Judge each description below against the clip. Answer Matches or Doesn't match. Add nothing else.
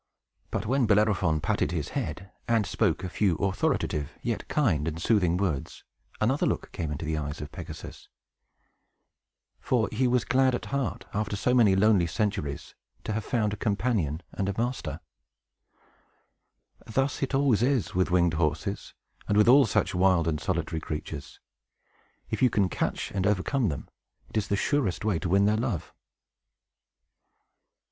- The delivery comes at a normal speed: Matches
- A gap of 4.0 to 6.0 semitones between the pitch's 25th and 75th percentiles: Matches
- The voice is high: Doesn't match